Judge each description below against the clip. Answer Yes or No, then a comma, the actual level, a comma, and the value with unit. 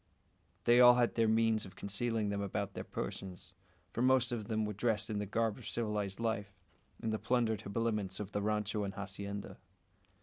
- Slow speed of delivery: No, average, 190 wpm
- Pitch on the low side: Yes, low, 105 Hz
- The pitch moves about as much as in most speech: No, narrow, 2.2 semitones